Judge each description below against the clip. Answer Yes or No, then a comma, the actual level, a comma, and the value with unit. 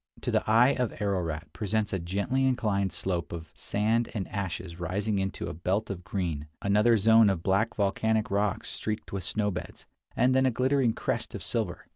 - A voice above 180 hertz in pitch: No, low, 100 Hz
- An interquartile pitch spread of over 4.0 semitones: No, average, 3.0 semitones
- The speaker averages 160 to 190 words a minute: Yes, average, 180 wpm